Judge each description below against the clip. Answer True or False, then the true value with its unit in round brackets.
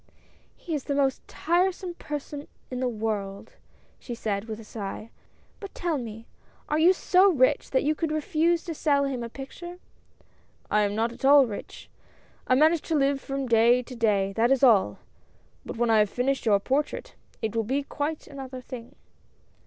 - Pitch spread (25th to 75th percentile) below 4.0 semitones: False (5.0 semitones)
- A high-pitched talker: True (260 Hz)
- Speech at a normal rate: True (195 wpm)